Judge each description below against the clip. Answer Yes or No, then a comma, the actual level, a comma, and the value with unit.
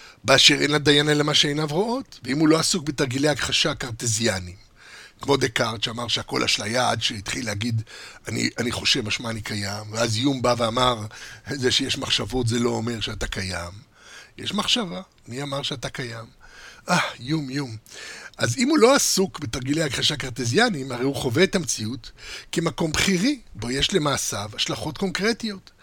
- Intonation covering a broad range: No, average, 4.9 semitones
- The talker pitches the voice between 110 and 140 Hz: Yes, low, 135 Hz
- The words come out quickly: Yes, fast, 165 wpm